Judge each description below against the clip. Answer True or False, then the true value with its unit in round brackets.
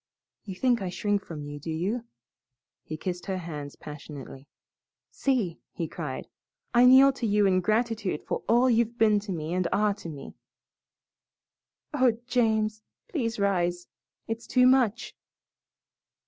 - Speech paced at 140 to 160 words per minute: True (150 wpm)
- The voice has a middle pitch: False (205 Hz)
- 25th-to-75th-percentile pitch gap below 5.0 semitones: False (5.4 semitones)